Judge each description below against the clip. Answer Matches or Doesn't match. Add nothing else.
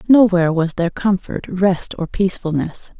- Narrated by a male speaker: Doesn't match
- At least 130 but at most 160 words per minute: Matches